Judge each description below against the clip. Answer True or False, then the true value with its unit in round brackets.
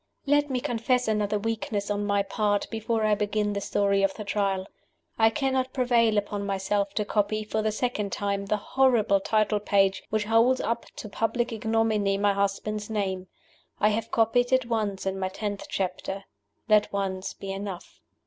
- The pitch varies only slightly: True (2.1 semitones)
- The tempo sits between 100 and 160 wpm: False (175 wpm)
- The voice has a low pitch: False (210 Hz)